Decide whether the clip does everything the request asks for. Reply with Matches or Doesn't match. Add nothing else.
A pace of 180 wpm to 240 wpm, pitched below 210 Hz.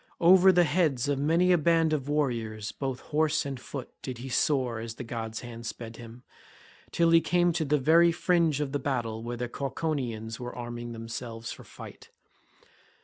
Matches